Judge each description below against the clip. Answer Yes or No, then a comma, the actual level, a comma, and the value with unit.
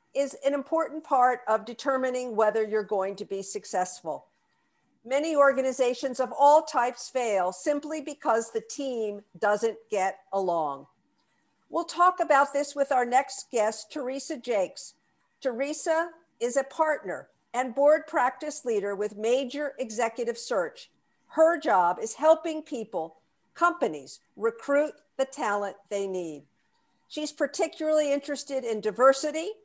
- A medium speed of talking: No, slow, 130 wpm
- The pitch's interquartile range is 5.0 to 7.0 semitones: Yes, wide, 5.5 semitones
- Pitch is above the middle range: Yes, very high, 260 Hz